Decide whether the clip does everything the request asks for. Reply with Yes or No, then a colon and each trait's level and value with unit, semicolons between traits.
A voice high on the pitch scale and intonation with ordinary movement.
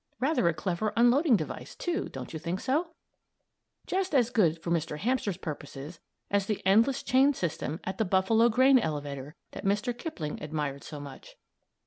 No: high, 195 Hz; wide, 8.0 semitones